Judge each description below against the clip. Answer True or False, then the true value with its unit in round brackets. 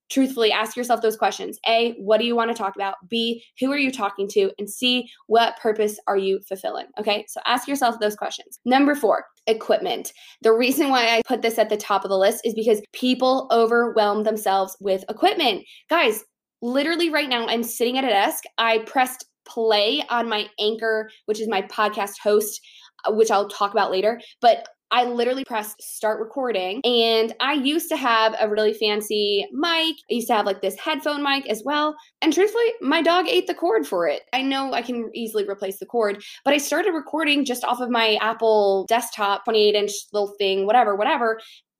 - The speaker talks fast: False (195 wpm)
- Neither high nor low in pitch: False (225 Hz)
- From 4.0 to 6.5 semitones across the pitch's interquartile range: False (3.6 semitones)